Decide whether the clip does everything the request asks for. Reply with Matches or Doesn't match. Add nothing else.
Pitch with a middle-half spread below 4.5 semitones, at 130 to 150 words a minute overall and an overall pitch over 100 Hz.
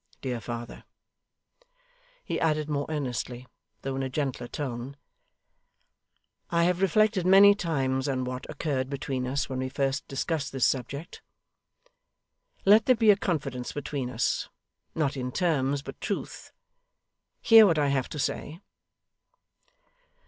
Matches